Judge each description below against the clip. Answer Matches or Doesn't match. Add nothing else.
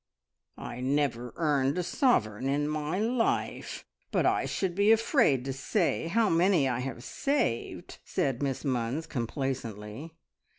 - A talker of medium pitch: Matches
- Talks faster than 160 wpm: Doesn't match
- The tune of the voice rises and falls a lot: Matches